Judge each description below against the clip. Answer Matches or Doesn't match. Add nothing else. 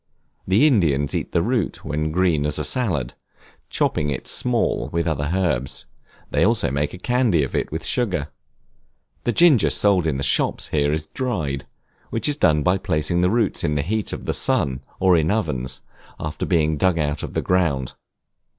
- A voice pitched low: Matches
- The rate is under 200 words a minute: Matches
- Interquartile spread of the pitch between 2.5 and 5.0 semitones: Doesn't match